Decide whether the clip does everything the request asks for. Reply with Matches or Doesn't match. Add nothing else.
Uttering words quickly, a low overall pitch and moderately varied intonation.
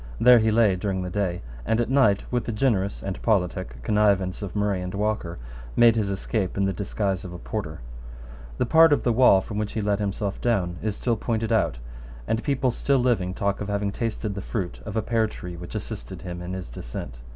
Matches